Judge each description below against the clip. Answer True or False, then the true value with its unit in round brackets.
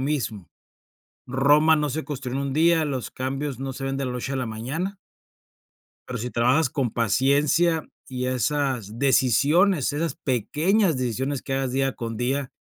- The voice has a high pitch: False (135 Hz)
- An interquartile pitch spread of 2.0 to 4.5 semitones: True (2.9 semitones)